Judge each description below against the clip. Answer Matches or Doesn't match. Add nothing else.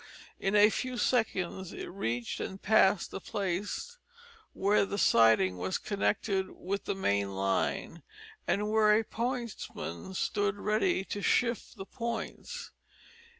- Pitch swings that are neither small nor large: Matches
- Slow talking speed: Matches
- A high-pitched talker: Matches